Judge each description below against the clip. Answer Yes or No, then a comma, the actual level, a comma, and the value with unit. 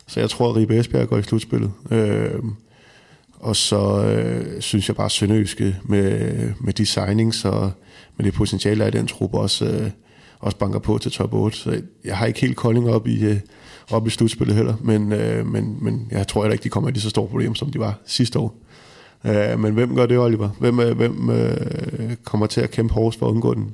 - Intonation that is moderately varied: No, narrow, 2.2 semitones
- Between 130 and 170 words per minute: No, average, 220 wpm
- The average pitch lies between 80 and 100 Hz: No, low, 110 Hz